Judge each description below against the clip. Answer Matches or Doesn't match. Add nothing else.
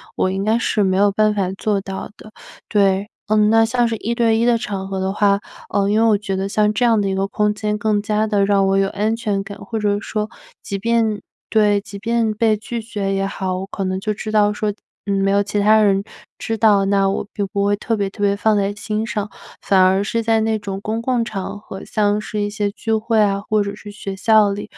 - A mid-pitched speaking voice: Doesn't match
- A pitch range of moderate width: Doesn't match